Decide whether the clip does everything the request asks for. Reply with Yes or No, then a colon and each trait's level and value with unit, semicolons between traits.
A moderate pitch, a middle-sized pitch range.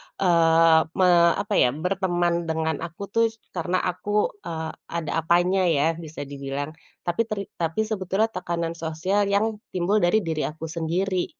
Yes: medium, 175 Hz; average, 3.1 semitones